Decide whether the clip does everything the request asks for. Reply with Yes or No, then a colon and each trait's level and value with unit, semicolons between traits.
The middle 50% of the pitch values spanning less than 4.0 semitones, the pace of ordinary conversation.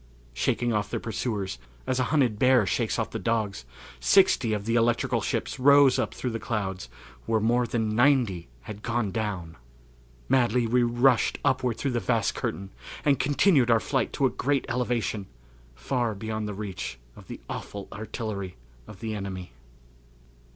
Yes: average, 3.4 semitones; average, 165 wpm